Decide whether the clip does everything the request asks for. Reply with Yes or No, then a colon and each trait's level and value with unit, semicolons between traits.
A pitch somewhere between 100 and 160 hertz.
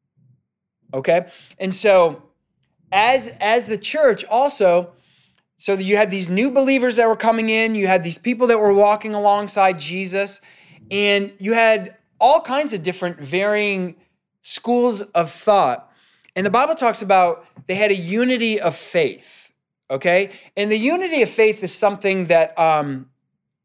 No: high, 200 Hz